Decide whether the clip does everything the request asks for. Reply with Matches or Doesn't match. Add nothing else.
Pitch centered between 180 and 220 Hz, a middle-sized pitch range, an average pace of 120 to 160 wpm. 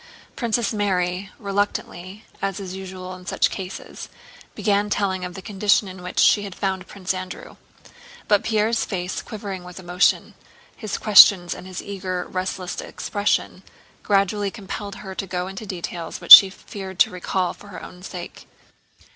Doesn't match